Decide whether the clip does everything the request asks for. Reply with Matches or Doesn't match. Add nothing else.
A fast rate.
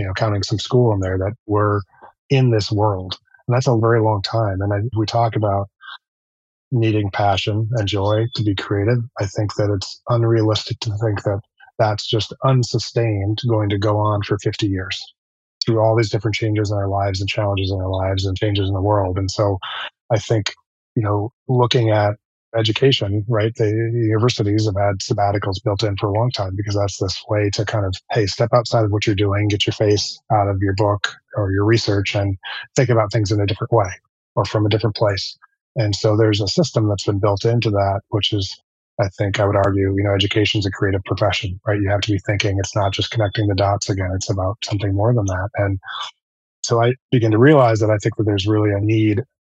Matches